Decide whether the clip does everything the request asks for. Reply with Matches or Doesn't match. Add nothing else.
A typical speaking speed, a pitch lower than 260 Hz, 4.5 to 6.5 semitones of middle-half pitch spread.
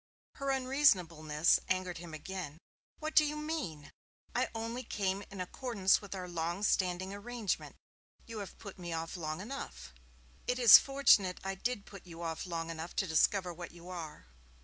Matches